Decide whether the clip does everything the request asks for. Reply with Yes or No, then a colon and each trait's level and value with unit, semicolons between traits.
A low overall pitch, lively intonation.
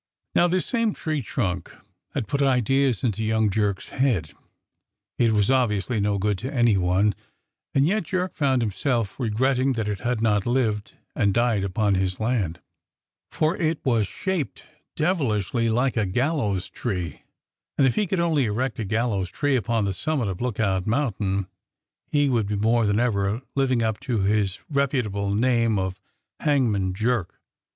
No: low, 115 Hz; average, 4.8 semitones